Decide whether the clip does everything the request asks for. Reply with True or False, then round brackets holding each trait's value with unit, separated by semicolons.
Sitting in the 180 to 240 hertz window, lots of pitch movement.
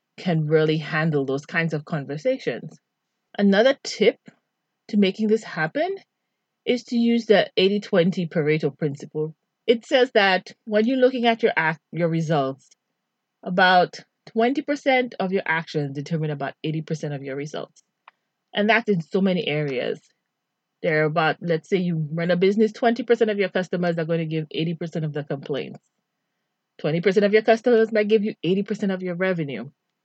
True (185 Hz; 5.7 semitones)